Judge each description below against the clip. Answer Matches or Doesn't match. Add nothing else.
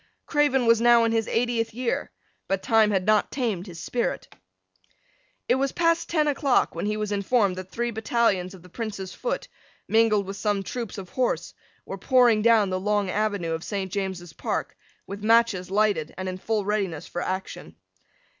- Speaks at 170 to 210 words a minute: Matches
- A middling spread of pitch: Matches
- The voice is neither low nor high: Doesn't match